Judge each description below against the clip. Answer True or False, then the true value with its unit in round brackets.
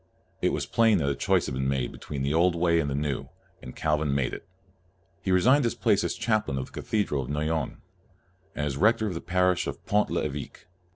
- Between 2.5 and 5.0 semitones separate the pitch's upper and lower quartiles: False (5.6 semitones)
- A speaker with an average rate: False (225 wpm)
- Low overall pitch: True (80 Hz)